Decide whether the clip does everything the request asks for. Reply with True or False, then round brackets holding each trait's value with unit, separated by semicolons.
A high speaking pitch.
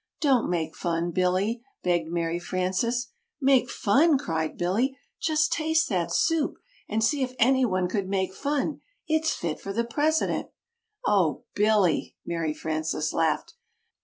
True (205 Hz)